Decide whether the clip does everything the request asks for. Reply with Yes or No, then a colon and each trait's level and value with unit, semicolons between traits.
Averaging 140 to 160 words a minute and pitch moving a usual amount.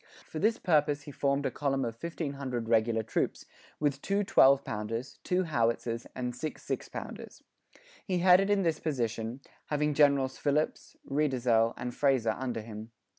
Yes: average, 155 wpm; average, 4.4 semitones